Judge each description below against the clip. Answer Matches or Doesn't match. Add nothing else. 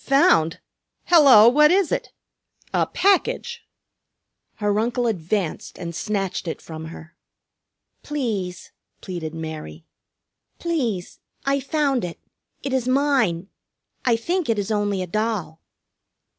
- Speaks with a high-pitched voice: Matches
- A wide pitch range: Matches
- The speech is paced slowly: Matches